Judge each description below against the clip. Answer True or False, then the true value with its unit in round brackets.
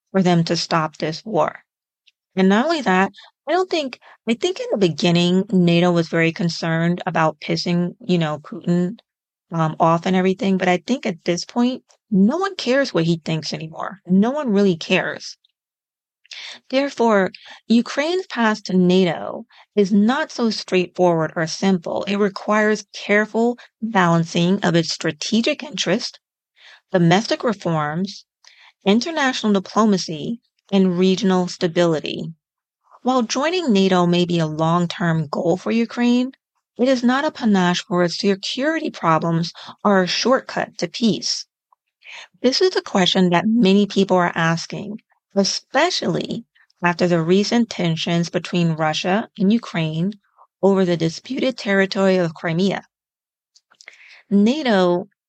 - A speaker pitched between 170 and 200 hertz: True (190 Hz)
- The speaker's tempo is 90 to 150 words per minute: True (135 wpm)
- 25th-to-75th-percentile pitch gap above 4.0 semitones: True (4.5 semitones)